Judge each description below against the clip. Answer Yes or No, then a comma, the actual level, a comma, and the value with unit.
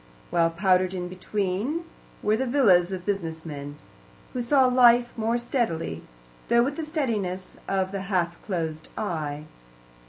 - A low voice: No, high, 190 Hz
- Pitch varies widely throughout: Yes, wide, 5.7 semitones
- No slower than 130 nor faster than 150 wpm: Yes, average, 145 wpm